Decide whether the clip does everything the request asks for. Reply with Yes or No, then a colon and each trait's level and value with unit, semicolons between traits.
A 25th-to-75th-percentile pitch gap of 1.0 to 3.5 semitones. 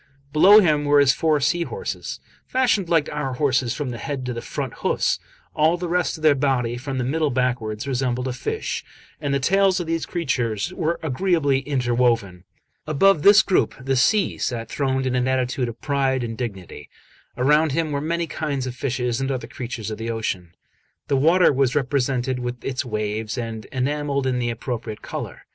No: average, 3.9 semitones